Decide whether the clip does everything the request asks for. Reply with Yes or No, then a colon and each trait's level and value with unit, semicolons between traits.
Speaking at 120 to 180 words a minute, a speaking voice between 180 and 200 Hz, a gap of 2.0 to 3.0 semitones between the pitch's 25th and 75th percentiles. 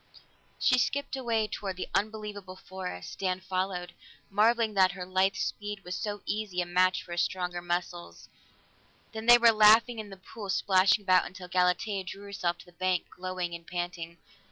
Yes: average, 175 wpm; medium, 185 Hz; average, 2.7 semitones